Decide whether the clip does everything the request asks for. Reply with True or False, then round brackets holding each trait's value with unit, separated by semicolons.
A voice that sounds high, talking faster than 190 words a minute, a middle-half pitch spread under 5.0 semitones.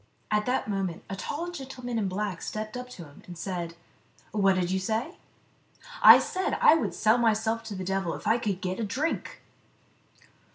True (210 Hz; 205 wpm; 4.4 semitones)